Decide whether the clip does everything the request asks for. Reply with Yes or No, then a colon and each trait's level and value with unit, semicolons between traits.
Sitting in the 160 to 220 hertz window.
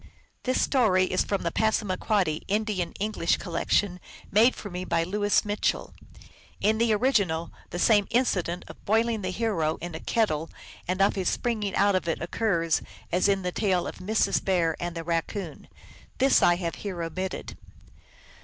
Yes: high, 190 Hz